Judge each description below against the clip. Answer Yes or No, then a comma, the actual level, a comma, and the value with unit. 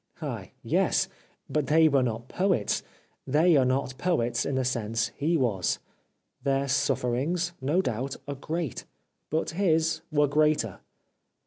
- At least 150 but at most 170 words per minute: No, slow, 135 wpm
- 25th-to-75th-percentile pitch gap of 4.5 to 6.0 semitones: No, average, 4.1 semitones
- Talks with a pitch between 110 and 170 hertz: Yes, medium, 140 Hz